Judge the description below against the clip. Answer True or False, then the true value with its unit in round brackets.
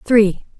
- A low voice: False (215 Hz)